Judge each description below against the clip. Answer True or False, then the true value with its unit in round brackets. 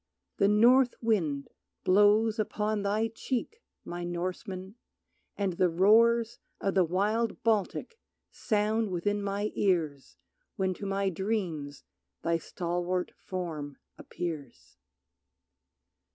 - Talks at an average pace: False (105 wpm)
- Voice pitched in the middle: False (195 Hz)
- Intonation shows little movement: False (3.7 semitones)